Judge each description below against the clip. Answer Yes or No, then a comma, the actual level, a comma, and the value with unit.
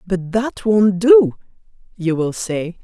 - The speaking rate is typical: Yes, average, 150 wpm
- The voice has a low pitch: No, high, 195 Hz